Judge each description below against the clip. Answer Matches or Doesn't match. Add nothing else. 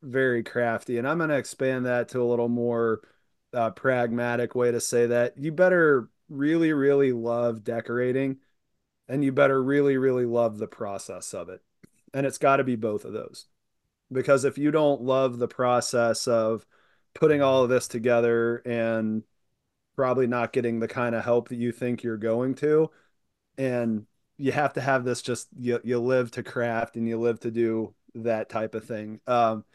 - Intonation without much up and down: Matches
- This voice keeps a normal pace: Matches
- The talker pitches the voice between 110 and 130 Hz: Matches